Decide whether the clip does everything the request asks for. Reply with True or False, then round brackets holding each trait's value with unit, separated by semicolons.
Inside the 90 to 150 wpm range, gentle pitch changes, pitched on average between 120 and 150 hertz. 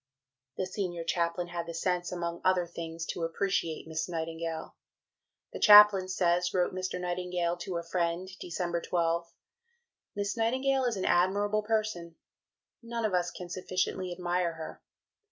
False (145 wpm; 1.8 semitones; 180 Hz)